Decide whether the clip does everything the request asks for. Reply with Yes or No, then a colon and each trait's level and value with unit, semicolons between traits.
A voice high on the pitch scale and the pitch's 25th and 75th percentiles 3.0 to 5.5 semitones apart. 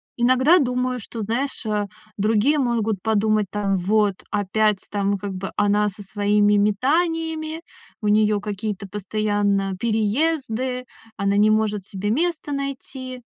Yes: high, 215 Hz; average, 3.7 semitones